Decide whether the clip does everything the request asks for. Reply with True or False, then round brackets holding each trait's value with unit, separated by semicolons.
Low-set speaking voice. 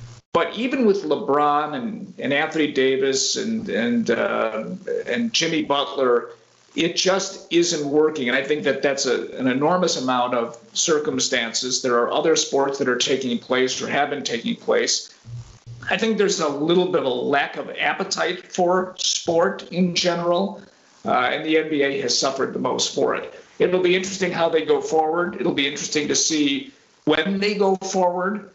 False (170 Hz)